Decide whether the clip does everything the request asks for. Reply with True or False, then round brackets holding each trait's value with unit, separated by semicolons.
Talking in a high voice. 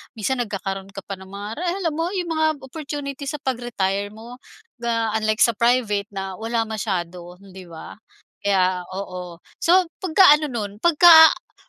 True (220 Hz)